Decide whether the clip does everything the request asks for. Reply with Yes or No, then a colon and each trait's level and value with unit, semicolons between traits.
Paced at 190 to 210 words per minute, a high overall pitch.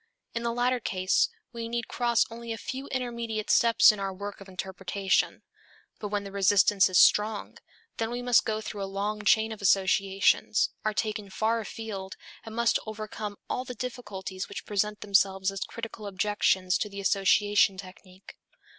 No: average, 170 wpm; high, 210 Hz